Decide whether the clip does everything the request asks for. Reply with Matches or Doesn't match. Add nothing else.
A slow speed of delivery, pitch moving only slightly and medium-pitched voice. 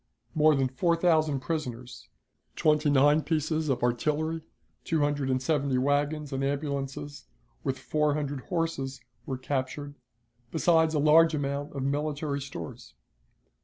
Matches